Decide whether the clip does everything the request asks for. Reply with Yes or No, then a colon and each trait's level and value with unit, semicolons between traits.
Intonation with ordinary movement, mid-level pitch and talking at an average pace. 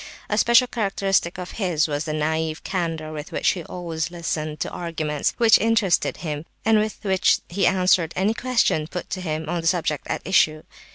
Yes: average, 3.7 semitones; medium, 175 Hz; average, 185 wpm